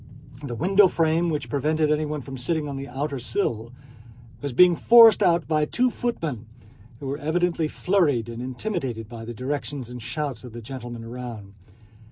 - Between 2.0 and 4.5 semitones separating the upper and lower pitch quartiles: No, average, 5.2 semitones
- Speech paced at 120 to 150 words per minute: No, average, 170 wpm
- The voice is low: No, medium, 145 Hz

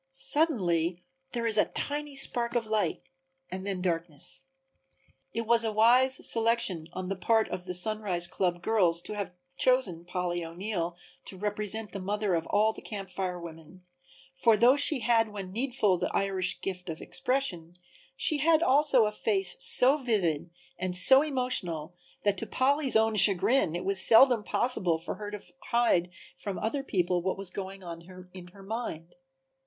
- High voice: Yes, high, 200 Hz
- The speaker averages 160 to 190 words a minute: Yes, average, 170 wpm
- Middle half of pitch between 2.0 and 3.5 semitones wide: No, average, 4.7 semitones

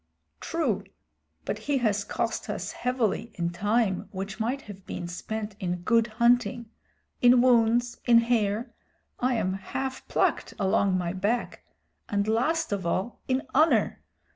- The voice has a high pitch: Yes, high, 225 Hz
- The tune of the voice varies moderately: Yes, average, 3.8 semitones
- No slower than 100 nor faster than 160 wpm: Yes, average, 140 wpm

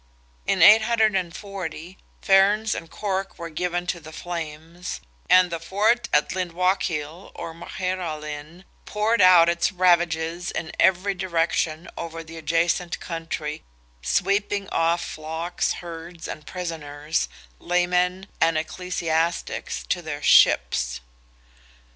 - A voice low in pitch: No, medium, 170 Hz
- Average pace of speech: No, slow, 110 wpm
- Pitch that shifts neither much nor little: No, narrow, 2.3 semitones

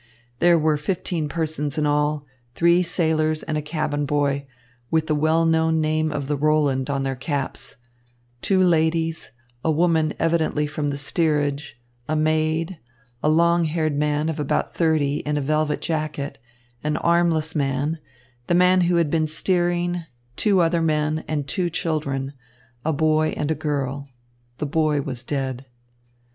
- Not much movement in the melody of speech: Yes, narrow, 1.9 semitones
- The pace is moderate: Yes, average, 155 wpm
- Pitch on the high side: No, medium, 155 Hz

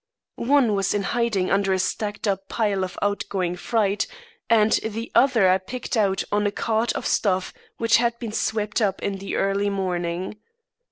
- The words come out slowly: No, average, 175 wpm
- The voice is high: Yes, high, 205 Hz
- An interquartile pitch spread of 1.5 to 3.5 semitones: Yes, narrow, 2.5 semitones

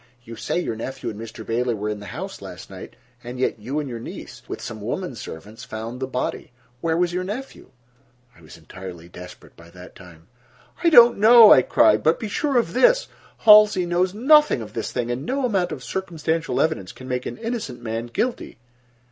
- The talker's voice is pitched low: Yes, low, 130 Hz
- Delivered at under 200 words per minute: No, fast, 205 wpm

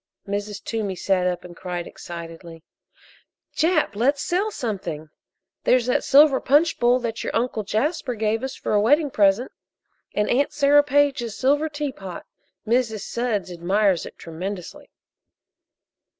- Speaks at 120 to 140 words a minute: Yes, slow, 135 wpm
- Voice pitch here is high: Yes, high, 225 Hz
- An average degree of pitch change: No, wide, 6.3 semitones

